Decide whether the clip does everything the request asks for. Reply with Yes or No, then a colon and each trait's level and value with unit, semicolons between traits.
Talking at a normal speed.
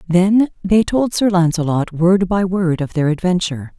Yes: average, 175 wpm